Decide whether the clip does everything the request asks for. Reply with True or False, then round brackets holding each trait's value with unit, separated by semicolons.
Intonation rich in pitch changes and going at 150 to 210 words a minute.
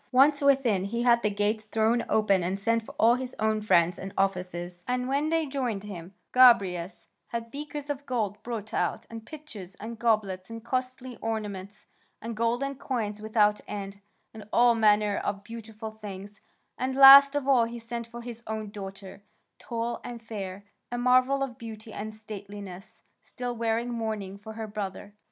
False (3.1 semitones; 170 wpm)